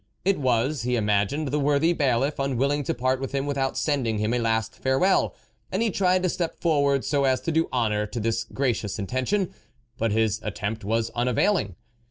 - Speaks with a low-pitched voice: Yes, low, 130 Hz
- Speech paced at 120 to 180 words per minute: No, average, 195 wpm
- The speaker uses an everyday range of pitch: Yes, average, 4.5 semitones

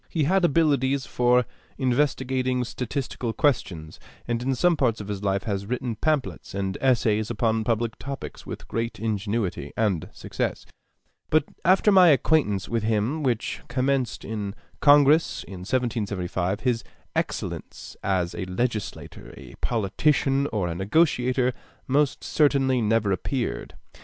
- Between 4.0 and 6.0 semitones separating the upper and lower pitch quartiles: Yes, average, 4.8 semitones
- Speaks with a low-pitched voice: Yes, low, 120 Hz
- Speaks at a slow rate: Yes, slow, 130 wpm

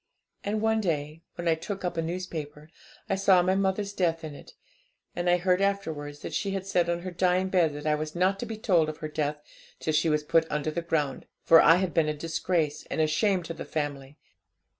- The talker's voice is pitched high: No, medium, 165 Hz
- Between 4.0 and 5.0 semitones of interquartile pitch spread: No, average, 3.5 semitones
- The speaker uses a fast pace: Yes, fast, 225 wpm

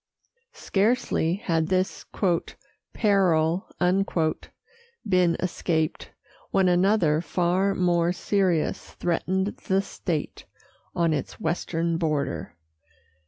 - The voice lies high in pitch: No, medium, 175 Hz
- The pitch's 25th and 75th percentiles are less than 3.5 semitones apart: Yes, average, 2.7 semitones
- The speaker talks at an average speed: No, slow, 80 wpm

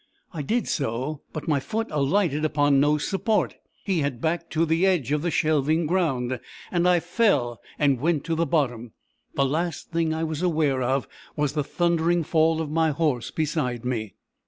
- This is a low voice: No, medium, 155 Hz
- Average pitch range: Yes, average, 3.3 semitones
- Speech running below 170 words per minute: No, average, 180 wpm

